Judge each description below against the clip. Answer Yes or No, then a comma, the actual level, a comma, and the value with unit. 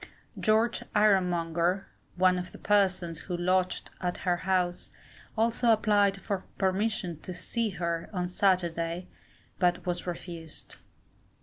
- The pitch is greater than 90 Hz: Yes, medium, 185 Hz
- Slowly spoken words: Yes, slow, 125 wpm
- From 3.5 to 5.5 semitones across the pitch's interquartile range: No, narrow, 2.4 semitones